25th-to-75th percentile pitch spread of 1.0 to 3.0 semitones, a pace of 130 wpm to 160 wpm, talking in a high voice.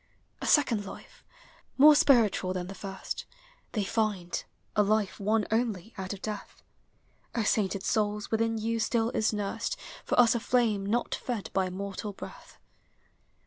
Yes: narrow, 2.4 semitones; average, 155 wpm; high, 210 Hz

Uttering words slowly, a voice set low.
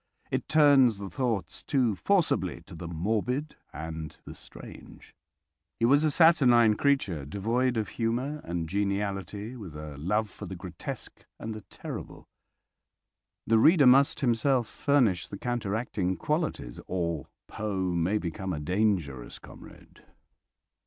Yes: slow, 130 wpm; low, 105 Hz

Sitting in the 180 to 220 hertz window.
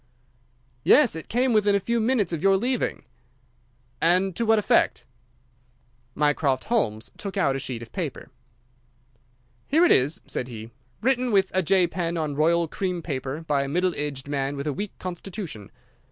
No: medium, 170 Hz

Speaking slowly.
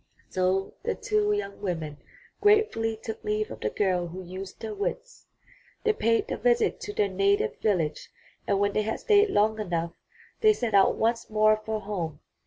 No: average, 180 wpm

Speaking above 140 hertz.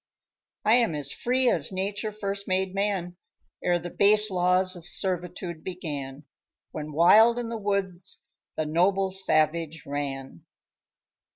Yes: medium, 185 Hz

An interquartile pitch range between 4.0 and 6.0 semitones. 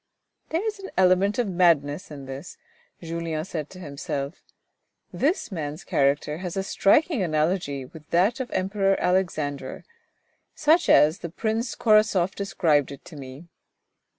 Yes: average, 5.0 semitones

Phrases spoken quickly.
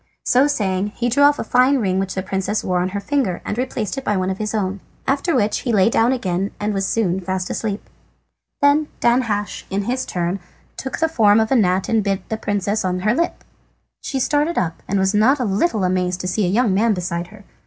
Yes: fast, 230 wpm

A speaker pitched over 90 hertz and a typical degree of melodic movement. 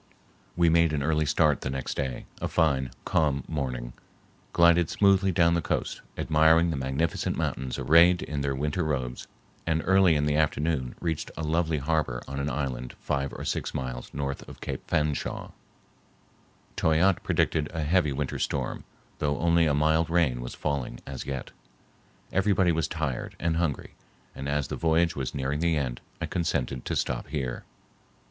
No: very low, 75 Hz; average, 3.4 semitones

